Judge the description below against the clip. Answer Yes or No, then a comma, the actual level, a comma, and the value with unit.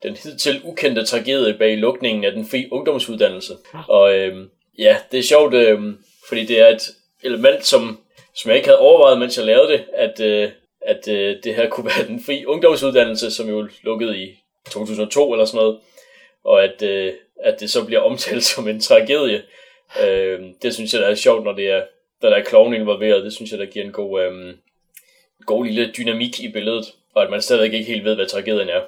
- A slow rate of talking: No, average, 210 wpm